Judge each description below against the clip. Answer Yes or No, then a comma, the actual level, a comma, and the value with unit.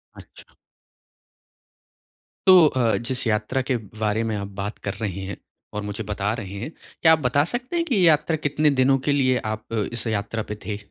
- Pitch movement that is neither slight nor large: No, wide, 5.7 semitones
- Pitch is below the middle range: Yes, low, 115 Hz